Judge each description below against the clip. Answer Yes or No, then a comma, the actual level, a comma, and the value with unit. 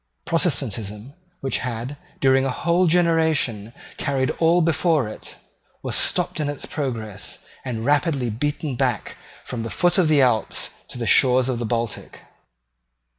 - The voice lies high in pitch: No, low, 135 Hz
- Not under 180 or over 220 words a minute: No, average, 145 wpm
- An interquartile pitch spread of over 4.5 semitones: Yes, average, 5.2 semitones